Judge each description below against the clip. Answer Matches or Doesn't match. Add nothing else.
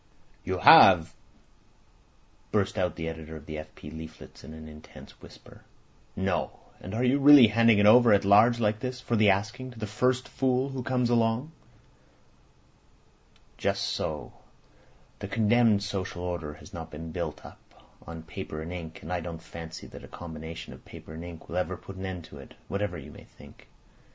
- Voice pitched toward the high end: Doesn't match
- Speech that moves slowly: Doesn't match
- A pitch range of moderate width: Doesn't match